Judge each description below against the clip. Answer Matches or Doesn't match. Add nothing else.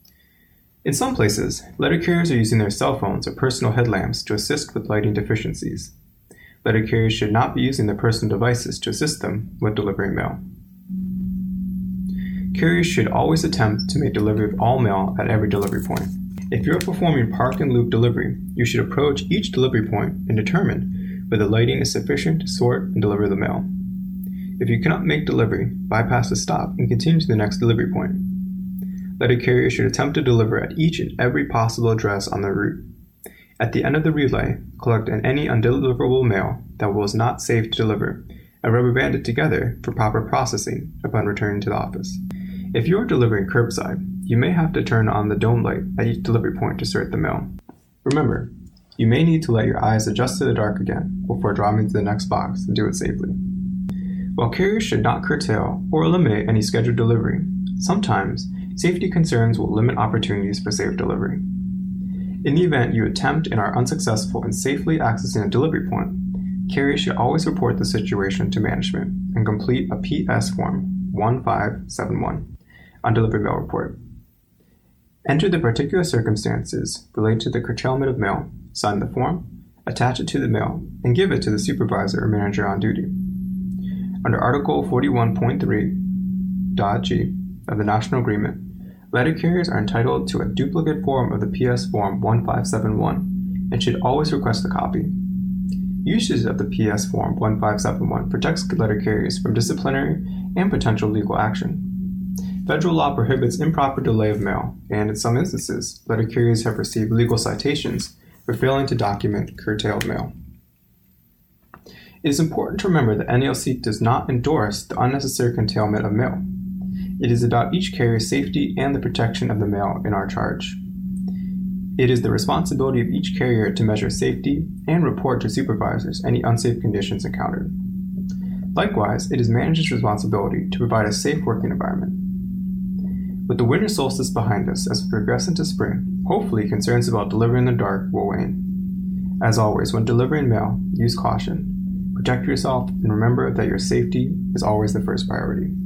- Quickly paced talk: Doesn't match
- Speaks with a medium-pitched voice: Doesn't match